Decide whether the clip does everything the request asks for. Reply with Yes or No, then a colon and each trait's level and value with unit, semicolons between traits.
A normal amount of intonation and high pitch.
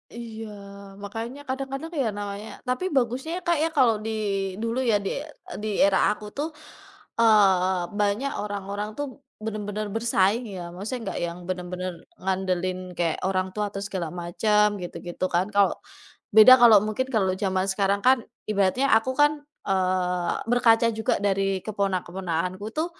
Yes: average, 3.5 semitones; high, 205 Hz